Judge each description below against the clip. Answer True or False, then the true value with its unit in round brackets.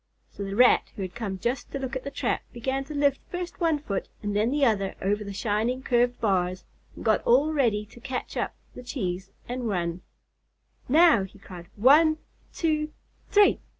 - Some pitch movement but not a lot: False (5.7 semitones)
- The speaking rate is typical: True (185 wpm)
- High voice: True (240 Hz)